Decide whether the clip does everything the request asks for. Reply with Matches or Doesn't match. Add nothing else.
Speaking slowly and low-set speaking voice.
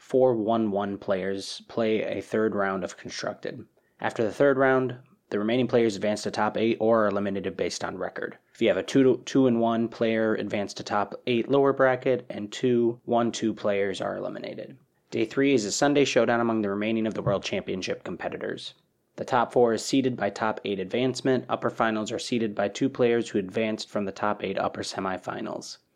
Doesn't match